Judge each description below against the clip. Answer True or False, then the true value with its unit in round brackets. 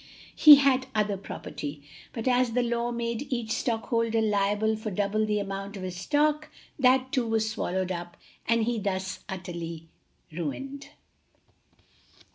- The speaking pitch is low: False (220 Hz)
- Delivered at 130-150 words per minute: True (140 wpm)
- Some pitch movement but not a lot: True (4.1 semitones)